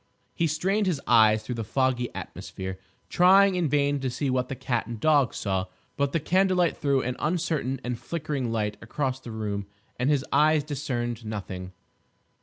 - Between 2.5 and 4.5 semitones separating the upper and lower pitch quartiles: No, average, 5.1 semitones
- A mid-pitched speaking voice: No, low, 130 Hz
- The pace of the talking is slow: No, average, 175 wpm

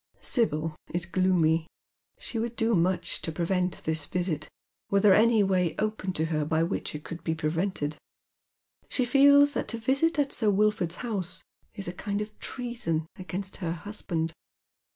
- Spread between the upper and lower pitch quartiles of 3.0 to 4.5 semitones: No, average, 5.0 semitones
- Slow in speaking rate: No, average, 165 wpm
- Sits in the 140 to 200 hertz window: Yes, medium, 185 Hz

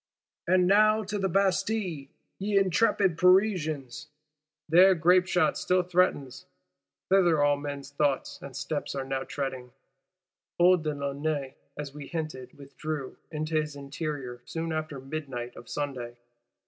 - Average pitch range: Yes, average, 4.8 semitones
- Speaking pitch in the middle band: Yes, medium, 155 Hz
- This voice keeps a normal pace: No, slow, 130 wpm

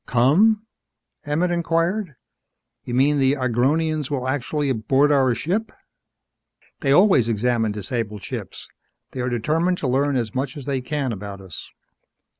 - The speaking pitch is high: No, low, 135 Hz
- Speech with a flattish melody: No, average, 4.3 semitones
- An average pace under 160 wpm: Yes, average, 145 wpm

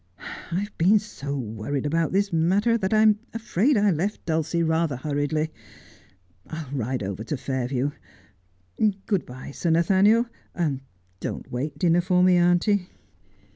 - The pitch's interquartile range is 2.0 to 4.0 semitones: No, wide, 5.6 semitones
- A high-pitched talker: No, medium, 165 Hz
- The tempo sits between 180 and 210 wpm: No, average, 140 wpm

